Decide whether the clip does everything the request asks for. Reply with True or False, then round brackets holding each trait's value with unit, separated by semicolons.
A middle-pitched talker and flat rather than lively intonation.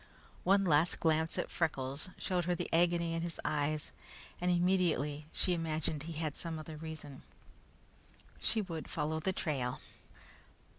True (160 Hz; 2.3 semitones)